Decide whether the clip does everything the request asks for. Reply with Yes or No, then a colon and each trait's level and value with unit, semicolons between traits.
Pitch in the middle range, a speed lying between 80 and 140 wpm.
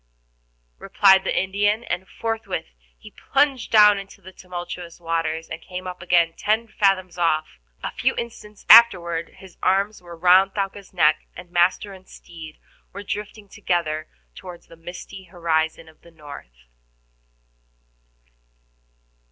Yes: medium, 180 Hz; slow, 135 wpm